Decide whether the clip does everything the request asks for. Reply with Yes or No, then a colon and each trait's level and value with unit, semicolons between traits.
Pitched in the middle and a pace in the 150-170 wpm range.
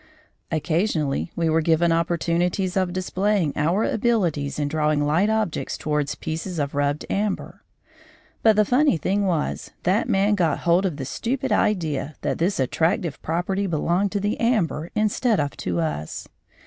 Yes: medium, 175 Hz; average, 155 wpm